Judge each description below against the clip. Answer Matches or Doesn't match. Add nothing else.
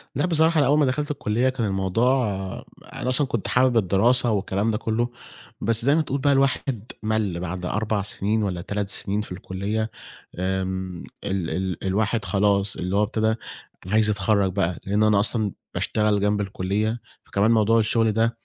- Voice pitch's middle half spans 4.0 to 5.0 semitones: Doesn't match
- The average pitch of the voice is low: Matches